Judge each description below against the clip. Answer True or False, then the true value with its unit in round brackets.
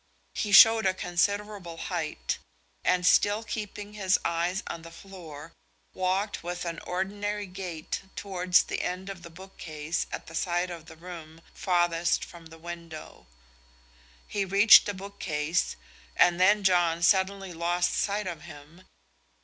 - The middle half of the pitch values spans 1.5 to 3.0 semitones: True (2.7 semitones)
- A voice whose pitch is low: False (180 Hz)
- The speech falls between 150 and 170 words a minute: False (140 wpm)